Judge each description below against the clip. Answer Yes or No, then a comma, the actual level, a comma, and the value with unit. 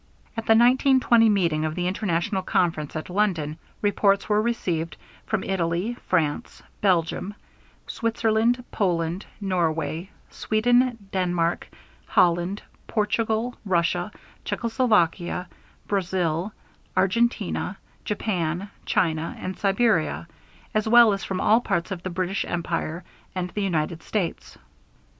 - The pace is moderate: No, slow, 110 wpm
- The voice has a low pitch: No, high, 190 Hz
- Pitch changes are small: No, average, 4.3 semitones